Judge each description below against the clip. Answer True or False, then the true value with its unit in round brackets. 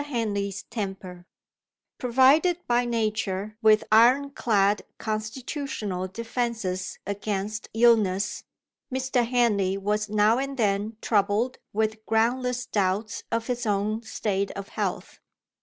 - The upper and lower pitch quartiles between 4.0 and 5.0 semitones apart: False (3.1 semitones)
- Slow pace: True (105 wpm)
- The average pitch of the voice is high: True (220 Hz)